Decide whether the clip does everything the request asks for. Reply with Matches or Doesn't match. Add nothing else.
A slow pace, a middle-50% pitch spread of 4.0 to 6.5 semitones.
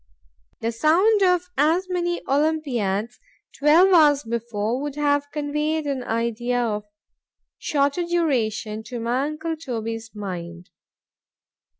Matches